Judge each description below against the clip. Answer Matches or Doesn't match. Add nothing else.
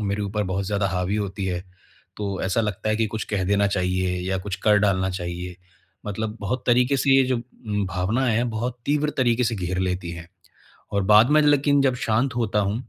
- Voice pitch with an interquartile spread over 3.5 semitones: Matches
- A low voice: Matches